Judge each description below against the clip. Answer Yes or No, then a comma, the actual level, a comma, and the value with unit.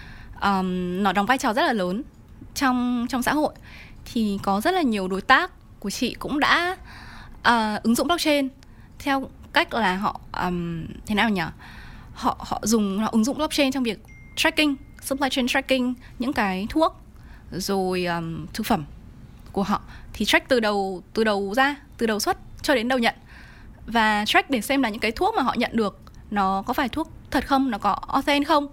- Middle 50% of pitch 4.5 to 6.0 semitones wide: Yes, wide, 5.5 semitones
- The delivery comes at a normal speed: Yes, average, 195 wpm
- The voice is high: Yes, high, 235 Hz